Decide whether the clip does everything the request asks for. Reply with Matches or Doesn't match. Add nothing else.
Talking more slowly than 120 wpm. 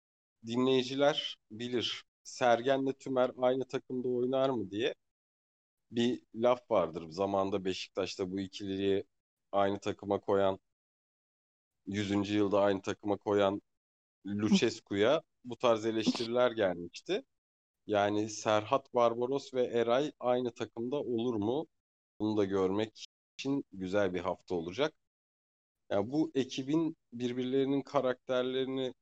Matches